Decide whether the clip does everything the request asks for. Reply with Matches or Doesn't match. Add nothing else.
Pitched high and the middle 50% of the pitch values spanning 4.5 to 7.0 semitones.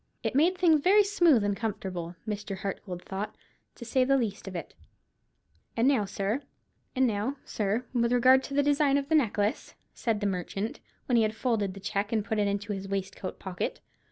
Matches